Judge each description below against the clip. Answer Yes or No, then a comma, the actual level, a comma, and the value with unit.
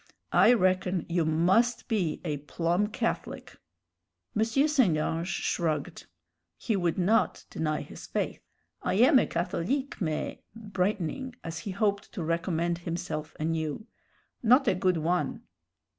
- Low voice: No, medium, 180 Hz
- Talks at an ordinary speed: No, slow, 130 wpm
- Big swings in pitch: No, average, 4.7 semitones